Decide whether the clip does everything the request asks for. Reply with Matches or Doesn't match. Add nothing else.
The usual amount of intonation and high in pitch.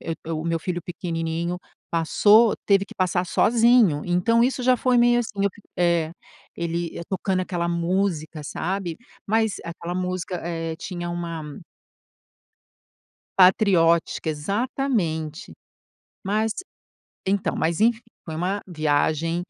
Doesn't match